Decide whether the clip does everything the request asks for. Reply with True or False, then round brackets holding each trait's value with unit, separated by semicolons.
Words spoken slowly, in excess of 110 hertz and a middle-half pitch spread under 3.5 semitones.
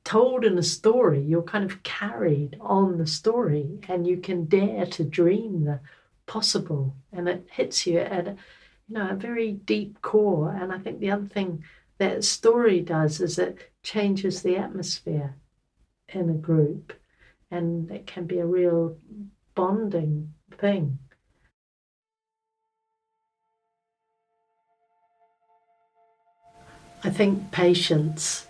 False (125 wpm; 185 Hz; 4.8 semitones)